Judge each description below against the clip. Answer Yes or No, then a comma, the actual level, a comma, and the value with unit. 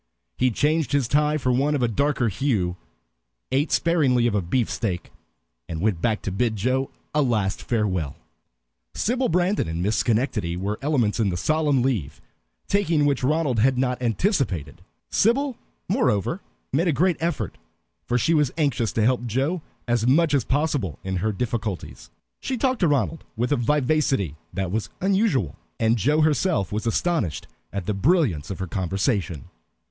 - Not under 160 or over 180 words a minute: Yes, average, 165 wpm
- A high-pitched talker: No, low, 125 Hz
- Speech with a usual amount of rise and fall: No, wide, 6.7 semitones